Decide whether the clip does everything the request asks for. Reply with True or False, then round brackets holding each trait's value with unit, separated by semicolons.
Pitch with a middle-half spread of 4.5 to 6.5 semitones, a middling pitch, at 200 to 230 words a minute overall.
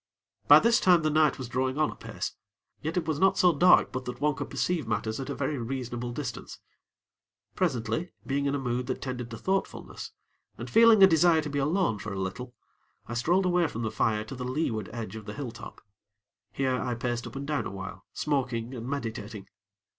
False (4.8 semitones; 130 Hz; 205 wpm)